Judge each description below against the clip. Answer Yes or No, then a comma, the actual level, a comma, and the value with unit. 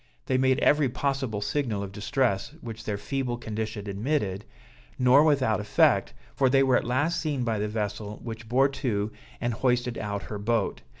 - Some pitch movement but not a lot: Yes, average, 4.1 semitones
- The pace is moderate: Yes, average, 175 wpm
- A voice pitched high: No, low, 120 Hz